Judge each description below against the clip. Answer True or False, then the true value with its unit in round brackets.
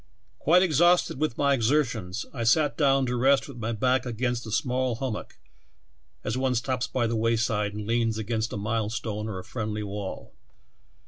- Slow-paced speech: False (180 wpm)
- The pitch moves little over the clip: False (3.2 semitones)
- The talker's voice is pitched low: True (120 Hz)